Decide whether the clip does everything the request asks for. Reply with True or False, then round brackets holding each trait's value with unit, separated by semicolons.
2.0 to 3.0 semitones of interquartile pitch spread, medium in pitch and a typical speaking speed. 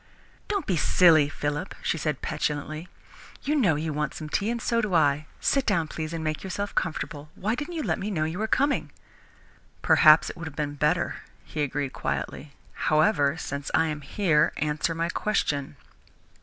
False (4.6 semitones; 155 Hz; 185 wpm)